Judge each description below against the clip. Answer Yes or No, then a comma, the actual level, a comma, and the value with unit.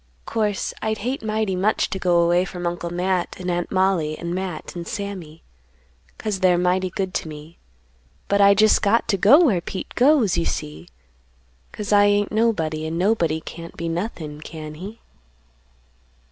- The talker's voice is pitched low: No, medium, 185 Hz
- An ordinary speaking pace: Yes, average, 170 wpm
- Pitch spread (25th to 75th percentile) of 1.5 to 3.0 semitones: No, average, 3.4 semitones